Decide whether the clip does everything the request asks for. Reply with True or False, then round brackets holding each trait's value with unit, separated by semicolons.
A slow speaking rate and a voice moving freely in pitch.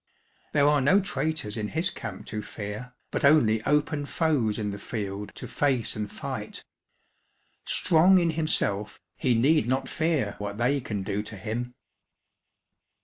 False (150 wpm; 6.2 semitones)